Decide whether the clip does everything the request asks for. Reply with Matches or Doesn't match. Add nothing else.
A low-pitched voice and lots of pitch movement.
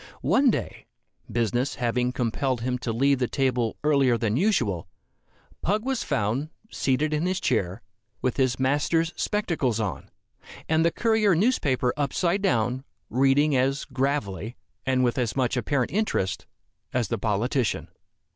Doesn't match